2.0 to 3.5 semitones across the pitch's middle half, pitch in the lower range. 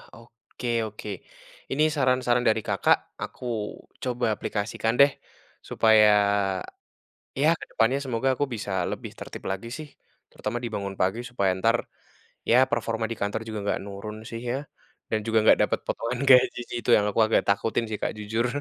Yes: narrow, 2.5 semitones; low, 115 Hz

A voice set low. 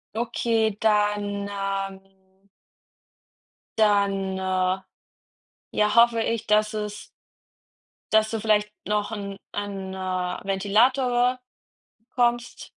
No: high, 210 Hz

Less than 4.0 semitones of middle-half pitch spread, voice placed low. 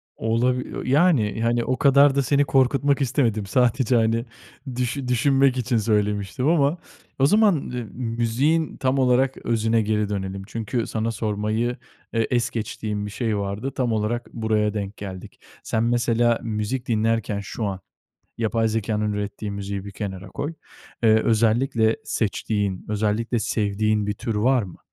Yes: average, 3.1 semitones; low, 115 Hz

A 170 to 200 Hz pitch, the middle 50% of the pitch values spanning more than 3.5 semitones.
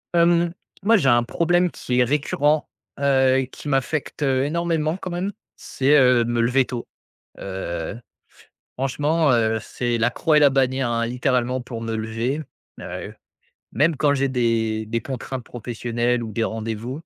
No: low, 130 Hz; average, 3.9 semitones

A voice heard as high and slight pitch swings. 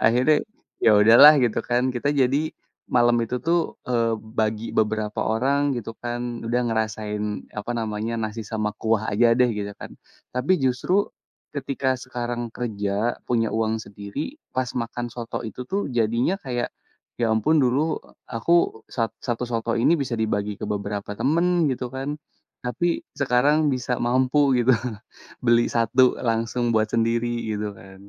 No: low, 120 Hz; narrow, 2.3 semitones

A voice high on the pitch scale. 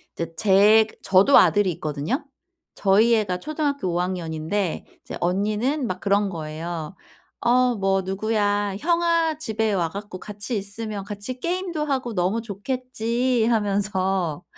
Yes: high, 205 Hz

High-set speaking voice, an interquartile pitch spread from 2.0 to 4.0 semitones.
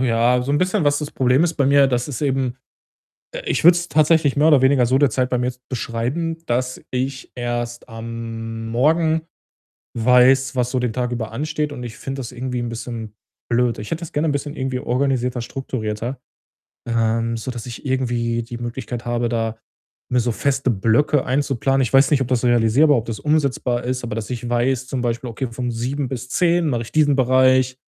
No: low, 125 Hz; narrow, 2.6 semitones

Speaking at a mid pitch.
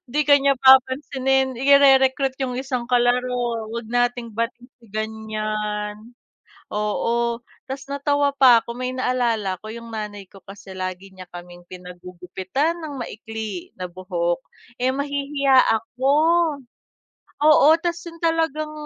No: high, 245 Hz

